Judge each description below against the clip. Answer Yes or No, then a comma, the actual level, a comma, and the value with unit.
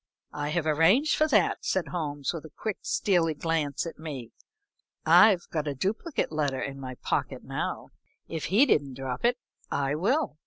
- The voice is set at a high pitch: No, medium, 160 Hz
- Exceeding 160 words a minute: Yes, average, 170 wpm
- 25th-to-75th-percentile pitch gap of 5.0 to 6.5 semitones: Yes, wide, 5.5 semitones